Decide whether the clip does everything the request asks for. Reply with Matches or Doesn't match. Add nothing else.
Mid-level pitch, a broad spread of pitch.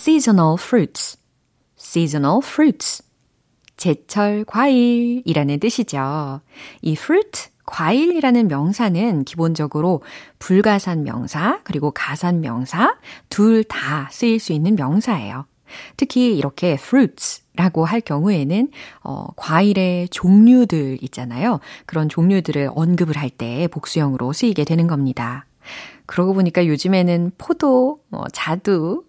Matches